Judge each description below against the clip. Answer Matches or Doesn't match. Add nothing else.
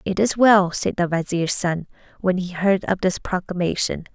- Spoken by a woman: Matches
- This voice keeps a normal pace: Matches